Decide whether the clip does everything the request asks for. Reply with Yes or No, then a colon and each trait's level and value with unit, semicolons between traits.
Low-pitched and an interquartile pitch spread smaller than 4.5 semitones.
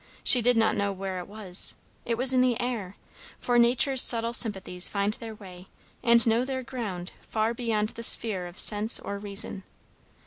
No: high, 220 Hz; average, 3.2 semitones